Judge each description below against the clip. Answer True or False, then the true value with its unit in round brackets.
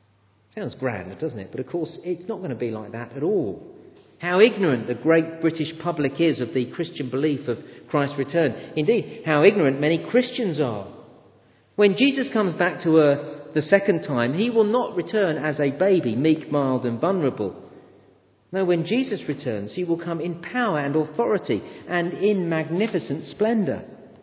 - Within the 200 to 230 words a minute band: False (175 wpm)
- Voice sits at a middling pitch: True (165 Hz)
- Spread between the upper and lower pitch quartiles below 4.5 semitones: False (5.3 semitones)